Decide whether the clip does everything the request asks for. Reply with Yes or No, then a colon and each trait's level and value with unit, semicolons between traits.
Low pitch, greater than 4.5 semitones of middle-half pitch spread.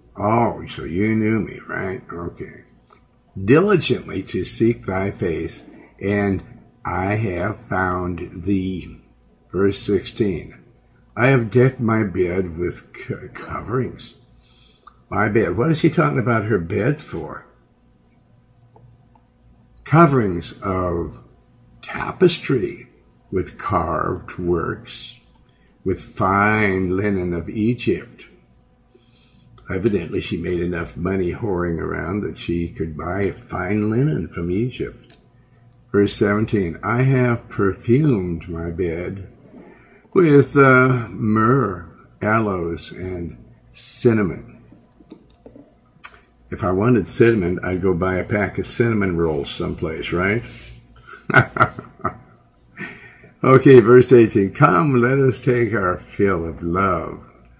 Yes: low, 100 Hz; average, 5.3 semitones